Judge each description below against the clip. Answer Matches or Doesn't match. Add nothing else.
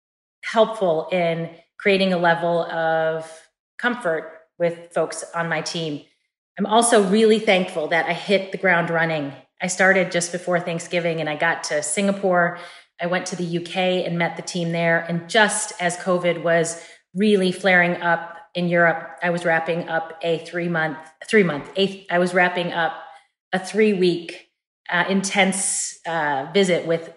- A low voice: Doesn't match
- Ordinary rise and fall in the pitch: Doesn't match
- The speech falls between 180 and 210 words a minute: Doesn't match